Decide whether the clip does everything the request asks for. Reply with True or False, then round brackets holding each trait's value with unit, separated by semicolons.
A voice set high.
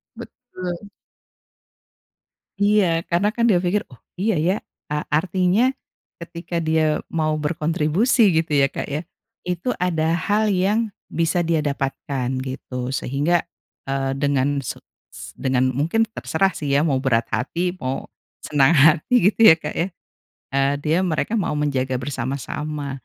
False (155 Hz)